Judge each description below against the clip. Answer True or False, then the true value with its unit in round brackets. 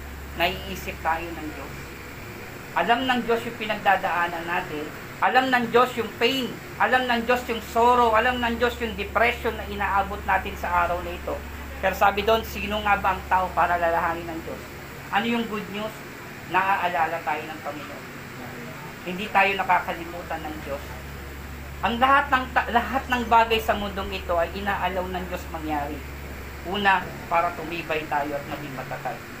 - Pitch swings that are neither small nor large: False (6.9 semitones)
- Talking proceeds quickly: True (160 wpm)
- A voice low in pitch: False (185 Hz)